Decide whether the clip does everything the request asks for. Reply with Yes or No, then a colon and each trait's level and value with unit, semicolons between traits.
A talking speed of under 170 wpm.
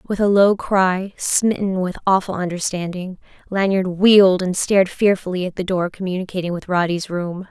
Yes: average, 160 wpm